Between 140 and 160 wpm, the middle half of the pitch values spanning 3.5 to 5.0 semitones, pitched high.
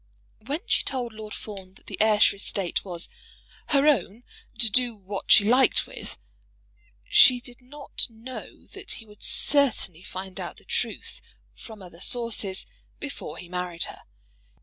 Yes: average, 150 wpm; average, 4.7 semitones; high, 220 Hz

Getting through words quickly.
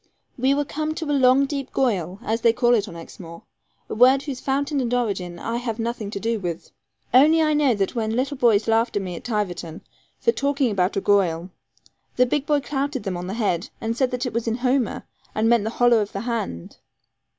Yes: fast, 225 wpm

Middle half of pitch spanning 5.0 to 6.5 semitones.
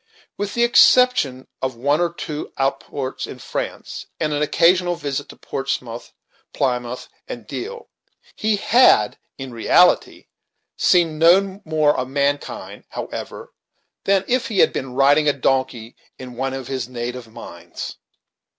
Yes: wide, 5.5 semitones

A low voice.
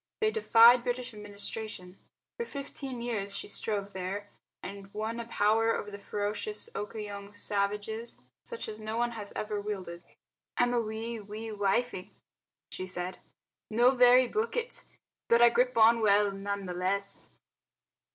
No: high, 215 Hz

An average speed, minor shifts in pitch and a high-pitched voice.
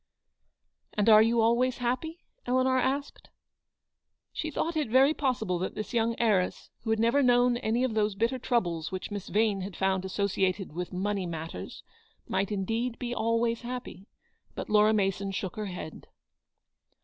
No: average, 160 wpm; average, 4.1 semitones; high, 220 Hz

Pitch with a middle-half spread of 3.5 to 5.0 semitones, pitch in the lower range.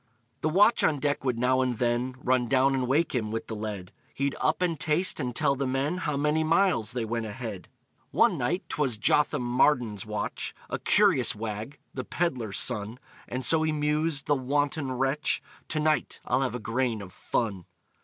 Yes: average, 4.4 semitones; low, 130 Hz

